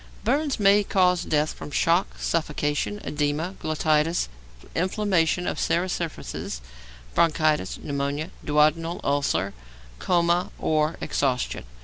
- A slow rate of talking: Yes, slow, 100 wpm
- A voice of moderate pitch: Yes, medium, 160 Hz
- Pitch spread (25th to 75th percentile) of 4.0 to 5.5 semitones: No, average, 3.2 semitones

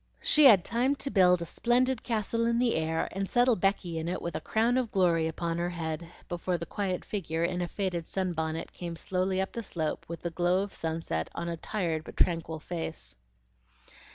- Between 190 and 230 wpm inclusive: Yes, fast, 205 wpm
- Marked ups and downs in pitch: No, average, 3.7 semitones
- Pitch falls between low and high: Yes, medium, 175 Hz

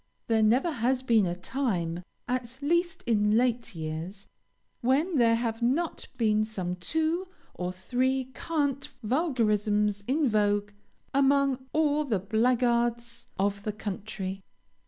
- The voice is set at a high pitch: Yes, high, 235 Hz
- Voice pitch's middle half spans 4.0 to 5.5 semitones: Yes, average, 4.4 semitones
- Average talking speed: No, slow, 125 wpm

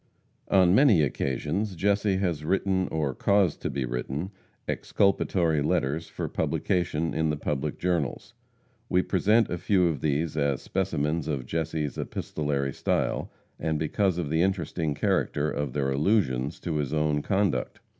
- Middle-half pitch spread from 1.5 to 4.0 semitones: No, average, 4.4 semitones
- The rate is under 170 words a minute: Yes, average, 145 wpm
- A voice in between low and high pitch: No, very low, 80 Hz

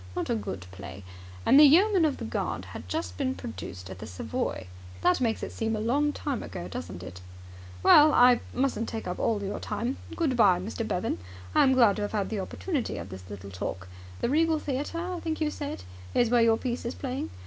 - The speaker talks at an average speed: No, fast, 220 wpm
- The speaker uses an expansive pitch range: Yes, wide, 8.1 semitones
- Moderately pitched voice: No, high, 230 Hz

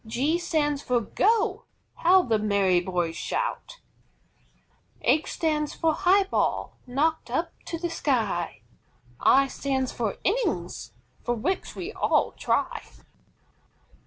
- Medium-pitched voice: No, very high, 290 Hz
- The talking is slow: Yes, slow, 120 wpm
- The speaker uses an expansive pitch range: Yes, wide, 7.9 semitones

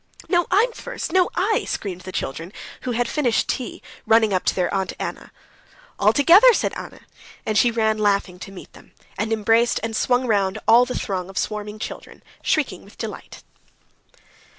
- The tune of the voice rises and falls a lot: No, average, 4.2 semitones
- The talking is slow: No, average, 175 wpm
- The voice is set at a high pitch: Yes, high, 220 Hz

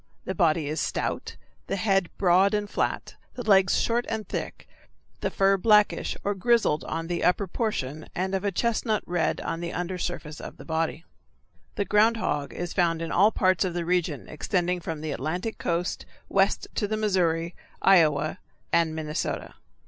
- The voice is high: No, medium, 180 Hz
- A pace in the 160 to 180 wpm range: Yes, average, 175 wpm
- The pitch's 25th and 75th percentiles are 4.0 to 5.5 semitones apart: No, average, 3.6 semitones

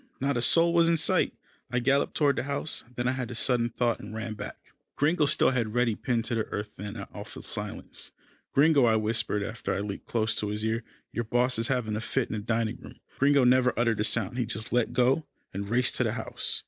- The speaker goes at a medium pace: No, fast, 240 wpm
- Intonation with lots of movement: No, average, 2.8 semitones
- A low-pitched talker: Yes, low, 120 Hz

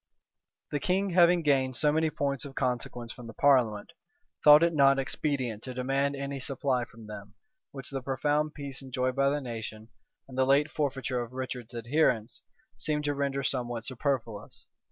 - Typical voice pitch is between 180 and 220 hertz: No, low, 135 Hz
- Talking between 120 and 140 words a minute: No, average, 170 wpm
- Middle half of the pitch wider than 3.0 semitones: No, average, 2.7 semitones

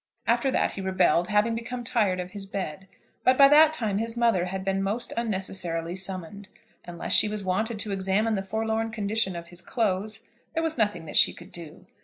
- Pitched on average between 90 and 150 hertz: No, high, 200 Hz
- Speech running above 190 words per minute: Yes, average, 200 wpm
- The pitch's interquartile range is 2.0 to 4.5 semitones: Yes, average, 3.2 semitones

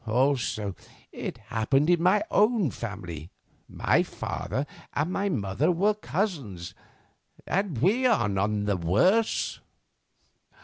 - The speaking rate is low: Yes, slow, 105 wpm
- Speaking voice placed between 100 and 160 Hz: Yes, medium, 140 Hz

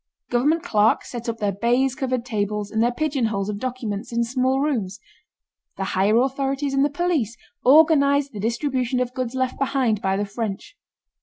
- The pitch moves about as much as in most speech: Yes, average, 4.1 semitones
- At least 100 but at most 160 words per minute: No, average, 170 wpm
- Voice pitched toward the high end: Yes, high, 245 Hz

